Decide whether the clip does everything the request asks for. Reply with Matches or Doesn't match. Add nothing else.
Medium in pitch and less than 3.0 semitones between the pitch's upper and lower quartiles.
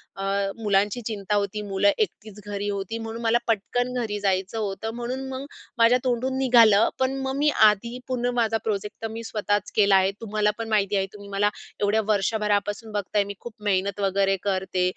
Doesn't match